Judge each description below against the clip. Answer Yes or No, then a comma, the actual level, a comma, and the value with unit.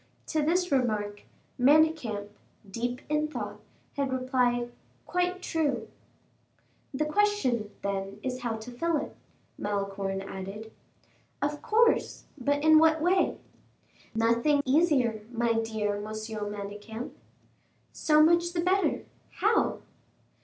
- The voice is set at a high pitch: Yes, very high, 250 Hz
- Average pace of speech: No, slow, 110 wpm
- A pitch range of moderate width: No, wide, 6.3 semitones